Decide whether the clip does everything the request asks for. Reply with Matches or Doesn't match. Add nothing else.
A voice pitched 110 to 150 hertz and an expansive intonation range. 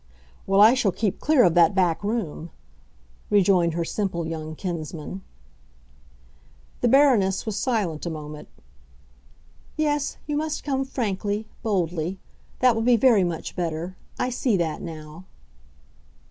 Doesn't match